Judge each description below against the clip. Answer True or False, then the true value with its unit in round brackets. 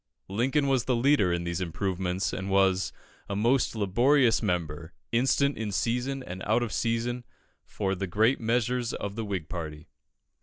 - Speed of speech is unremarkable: True (160 wpm)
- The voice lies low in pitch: True (105 Hz)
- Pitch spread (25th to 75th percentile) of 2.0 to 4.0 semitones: False (4.6 semitones)